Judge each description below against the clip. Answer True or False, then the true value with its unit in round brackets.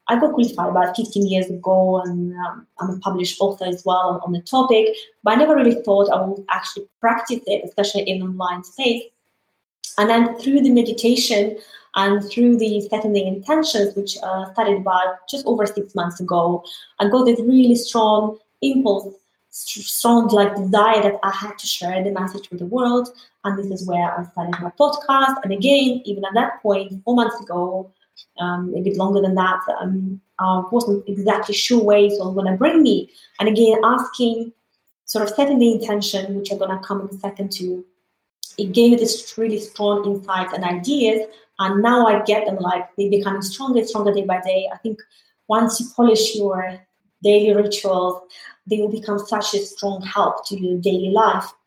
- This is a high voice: True (205 Hz)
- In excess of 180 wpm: True (190 wpm)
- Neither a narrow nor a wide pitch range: True (3.2 semitones)